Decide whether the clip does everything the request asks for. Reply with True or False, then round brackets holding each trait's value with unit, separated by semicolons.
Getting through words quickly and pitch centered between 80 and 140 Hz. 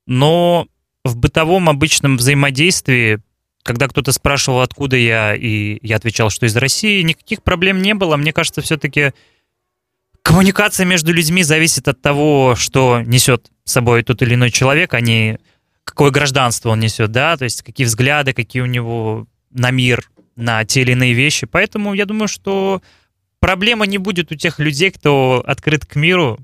True (165 wpm; 135 Hz)